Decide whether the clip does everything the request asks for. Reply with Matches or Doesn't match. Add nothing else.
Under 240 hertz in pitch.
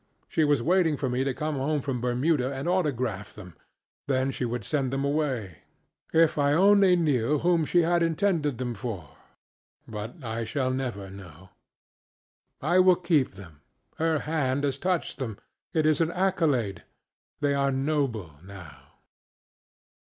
Matches